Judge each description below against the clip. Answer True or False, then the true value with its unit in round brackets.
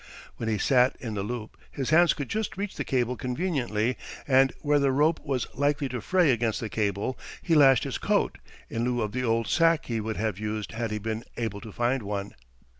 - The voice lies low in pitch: True (120 Hz)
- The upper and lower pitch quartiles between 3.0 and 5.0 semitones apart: True (4.2 semitones)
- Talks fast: True (215 wpm)